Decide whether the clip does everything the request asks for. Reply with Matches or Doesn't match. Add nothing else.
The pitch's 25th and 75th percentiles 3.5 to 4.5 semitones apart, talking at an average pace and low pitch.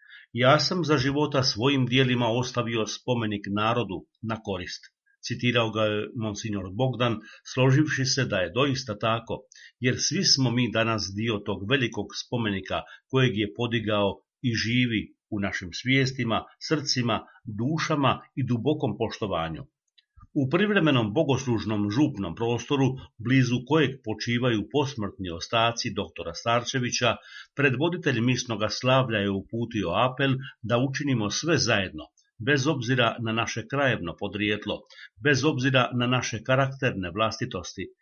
Matches